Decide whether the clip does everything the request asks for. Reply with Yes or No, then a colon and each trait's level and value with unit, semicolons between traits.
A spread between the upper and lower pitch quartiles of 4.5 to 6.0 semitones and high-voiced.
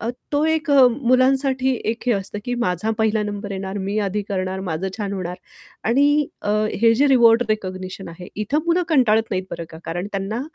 Yes: average, 5.0 semitones; high, 215 Hz